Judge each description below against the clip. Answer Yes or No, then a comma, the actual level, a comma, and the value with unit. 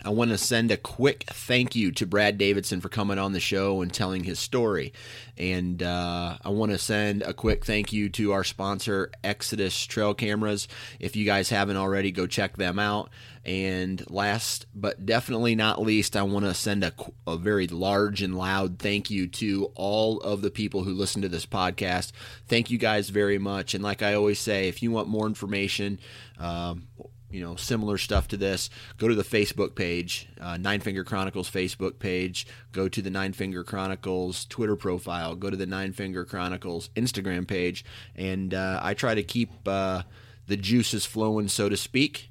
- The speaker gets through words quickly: No, average, 190 wpm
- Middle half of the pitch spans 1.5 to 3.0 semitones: Yes, narrow, 2.5 semitones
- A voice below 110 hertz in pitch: Yes, low, 100 Hz